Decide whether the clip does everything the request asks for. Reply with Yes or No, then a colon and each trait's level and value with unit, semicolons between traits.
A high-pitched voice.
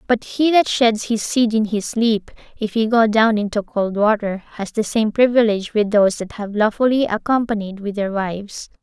Yes: high, 215 Hz